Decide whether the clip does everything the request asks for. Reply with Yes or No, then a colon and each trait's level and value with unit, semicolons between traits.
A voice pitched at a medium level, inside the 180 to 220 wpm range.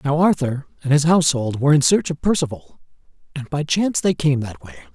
Yes: medium, 150 Hz; fast, 205 wpm